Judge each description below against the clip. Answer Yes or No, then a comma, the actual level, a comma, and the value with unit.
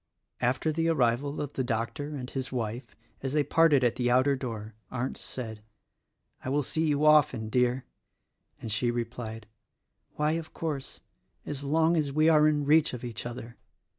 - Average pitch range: Yes, average, 3.9 semitones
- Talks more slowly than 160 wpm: No, average, 170 wpm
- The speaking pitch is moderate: No, low, 130 Hz